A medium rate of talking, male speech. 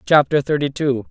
Yes: average, 165 wpm; male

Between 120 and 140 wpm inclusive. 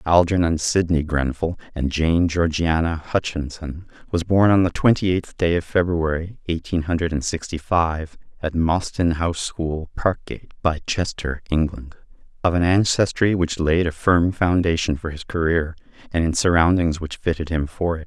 No: average, 160 wpm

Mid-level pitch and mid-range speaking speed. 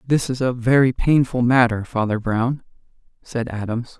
No: low, 120 Hz; average, 150 wpm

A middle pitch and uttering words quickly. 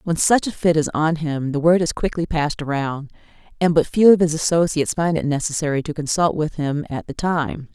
Yes: medium, 160 Hz; fast, 225 wpm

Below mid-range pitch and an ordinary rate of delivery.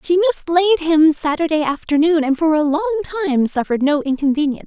No: very high, 320 Hz; average, 155 wpm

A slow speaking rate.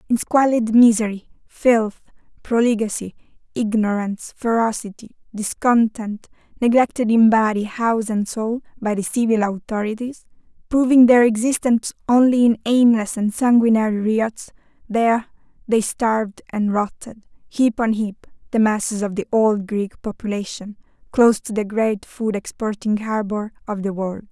Yes: slow, 130 wpm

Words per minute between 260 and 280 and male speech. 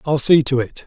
Yes: fast, 275 wpm; male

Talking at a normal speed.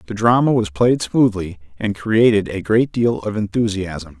Yes: average, 170 wpm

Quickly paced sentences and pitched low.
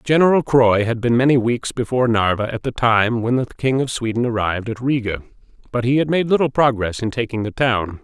Yes: fast, 215 wpm; low, 120 Hz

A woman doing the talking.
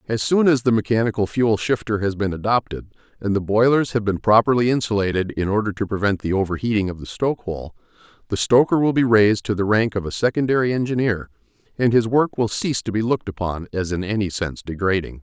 No: male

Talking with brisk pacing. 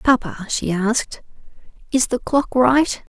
No: slow, 135 wpm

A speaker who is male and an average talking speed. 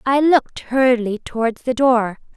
No: female; average, 155 wpm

